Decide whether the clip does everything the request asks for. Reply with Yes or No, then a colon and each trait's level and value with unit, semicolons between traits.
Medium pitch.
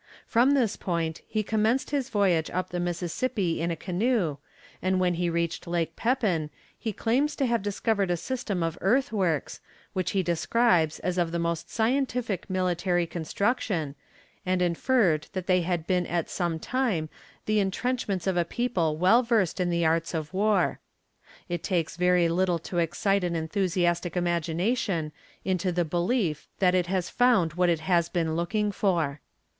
Yes: medium, 180 Hz